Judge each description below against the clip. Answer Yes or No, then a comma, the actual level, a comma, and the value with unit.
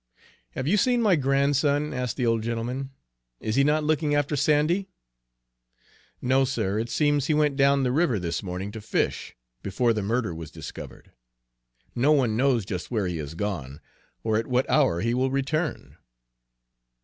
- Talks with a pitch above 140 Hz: No, low, 130 Hz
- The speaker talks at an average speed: Yes, average, 170 wpm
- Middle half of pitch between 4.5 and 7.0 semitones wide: Yes, average, 5.1 semitones